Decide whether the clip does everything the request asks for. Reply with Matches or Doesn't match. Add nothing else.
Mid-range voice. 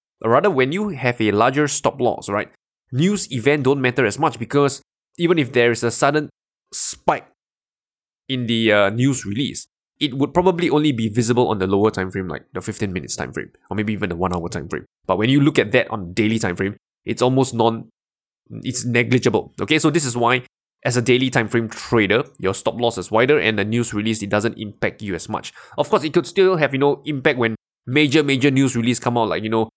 Doesn't match